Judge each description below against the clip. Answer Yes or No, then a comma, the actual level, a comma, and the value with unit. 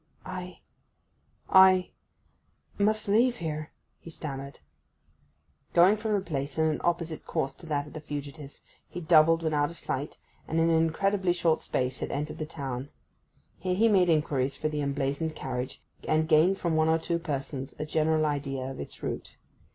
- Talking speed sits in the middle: Yes, average, 165 wpm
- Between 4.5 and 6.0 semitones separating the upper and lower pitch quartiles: No, average, 3.4 semitones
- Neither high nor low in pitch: Yes, medium, 160 Hz